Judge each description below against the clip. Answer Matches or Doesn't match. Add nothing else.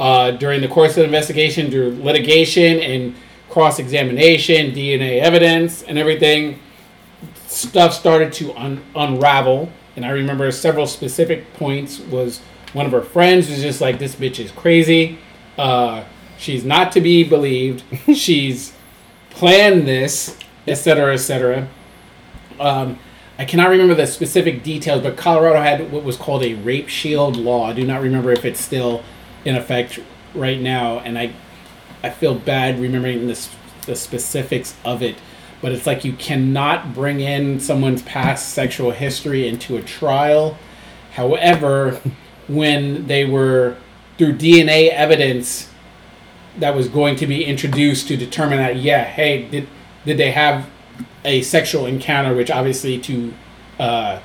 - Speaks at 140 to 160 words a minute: Matches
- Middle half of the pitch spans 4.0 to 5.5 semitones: Doesn't match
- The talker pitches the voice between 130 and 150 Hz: Matches